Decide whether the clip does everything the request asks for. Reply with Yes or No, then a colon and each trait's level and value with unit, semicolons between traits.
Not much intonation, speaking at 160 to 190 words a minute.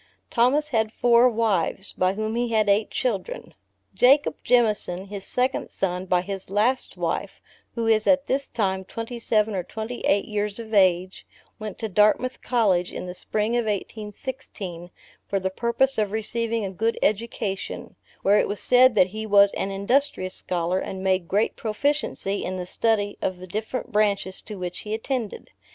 No: average, 3.4 semitones; average, 170 wpm